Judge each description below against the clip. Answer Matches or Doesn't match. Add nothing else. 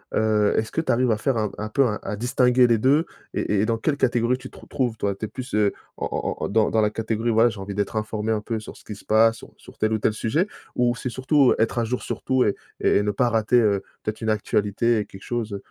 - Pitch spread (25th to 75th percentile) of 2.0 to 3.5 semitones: Matches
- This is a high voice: Doesn't match